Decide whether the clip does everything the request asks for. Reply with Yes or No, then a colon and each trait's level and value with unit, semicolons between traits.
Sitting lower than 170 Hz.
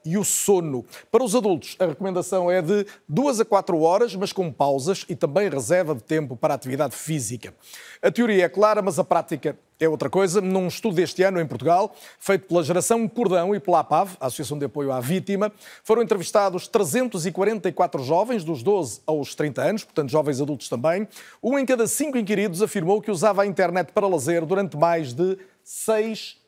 No: medium, 185 Hz